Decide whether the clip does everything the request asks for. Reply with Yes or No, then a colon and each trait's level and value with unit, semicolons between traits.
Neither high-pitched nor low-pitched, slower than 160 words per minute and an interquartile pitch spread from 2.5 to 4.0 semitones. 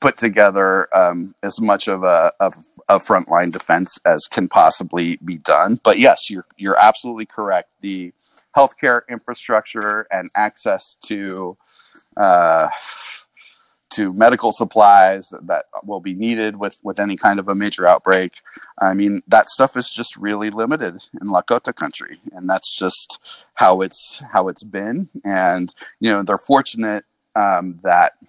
No: low, 100 Hz; average, 150 wpm; average, 2.9 semitones